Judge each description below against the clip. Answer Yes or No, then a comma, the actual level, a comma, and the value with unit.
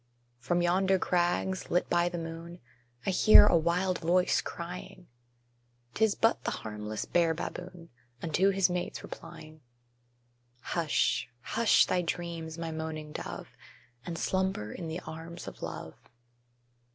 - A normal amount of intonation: No, narrow, 2.0 semitones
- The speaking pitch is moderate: Yes, medium, 175 Hz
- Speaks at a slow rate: Yes, slow, 130 wpm